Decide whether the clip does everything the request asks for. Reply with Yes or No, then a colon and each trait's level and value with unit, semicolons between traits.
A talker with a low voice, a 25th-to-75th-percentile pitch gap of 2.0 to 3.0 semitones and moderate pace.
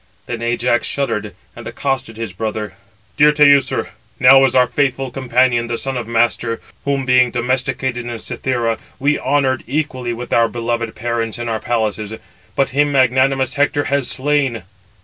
Yes: low, 125 Hz; narrow, 2.4 semitones; average, 155 wpm